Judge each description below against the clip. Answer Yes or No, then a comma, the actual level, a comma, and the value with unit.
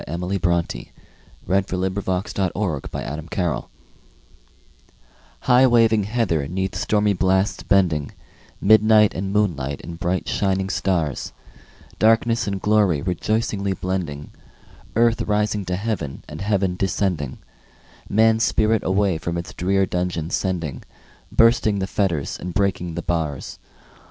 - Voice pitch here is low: Yes, very low, 95 Hz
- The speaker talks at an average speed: No, slow, 125 wpm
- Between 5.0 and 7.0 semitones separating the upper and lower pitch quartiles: No, average, 3.4 semitones